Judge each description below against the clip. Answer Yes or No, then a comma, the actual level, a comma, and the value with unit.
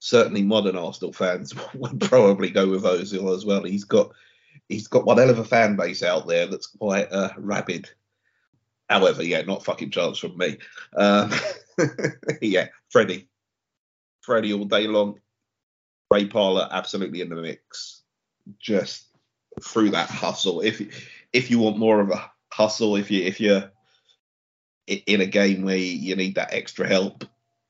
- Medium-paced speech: Yes, average, 155 wpm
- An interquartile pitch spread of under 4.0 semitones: Yes, narrow, 2.5 semitones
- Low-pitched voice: Yes, low, 100 Hz